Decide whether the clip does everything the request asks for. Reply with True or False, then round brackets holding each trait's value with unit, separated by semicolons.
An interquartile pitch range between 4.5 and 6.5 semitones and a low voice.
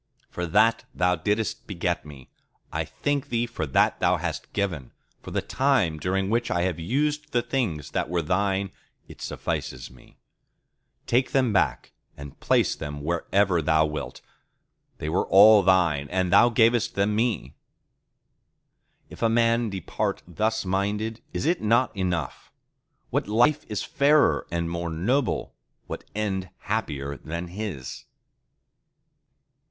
True (5.3 semitones; 100 Hz)